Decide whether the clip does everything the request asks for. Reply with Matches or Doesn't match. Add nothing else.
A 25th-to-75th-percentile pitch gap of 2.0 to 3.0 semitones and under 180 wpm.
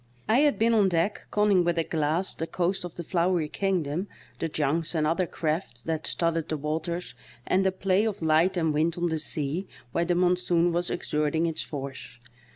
Doesn't match